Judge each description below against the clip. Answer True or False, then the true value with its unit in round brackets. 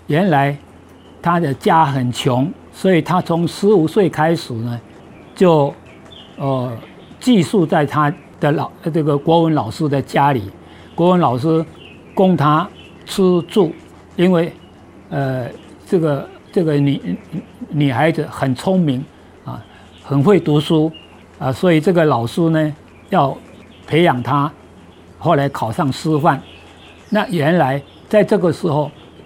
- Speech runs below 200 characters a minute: True (180 characters per minute)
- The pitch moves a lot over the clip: False (4.3 semitones)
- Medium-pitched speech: True (150 Hz)